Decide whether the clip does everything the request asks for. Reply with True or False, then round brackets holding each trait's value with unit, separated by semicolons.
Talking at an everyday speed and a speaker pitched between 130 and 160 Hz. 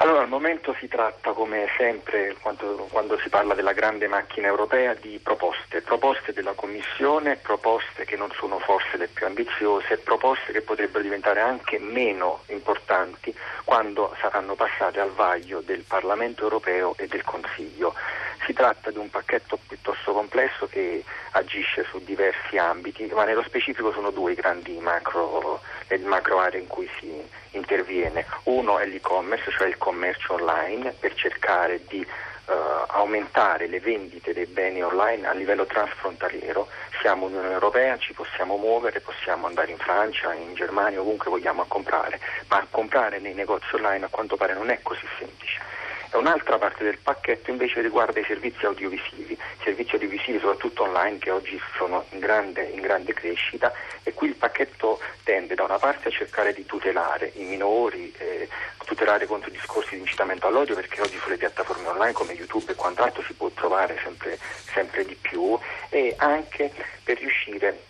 True (160 wpm; 135 Hz)